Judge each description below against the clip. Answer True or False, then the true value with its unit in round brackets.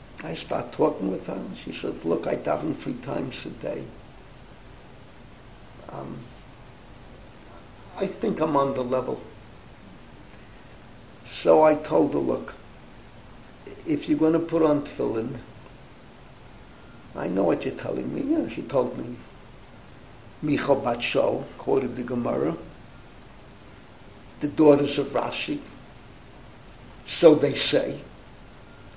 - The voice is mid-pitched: True (145 Hz)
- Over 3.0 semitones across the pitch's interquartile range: True (3.7 semitones)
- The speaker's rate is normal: False (115 wpm)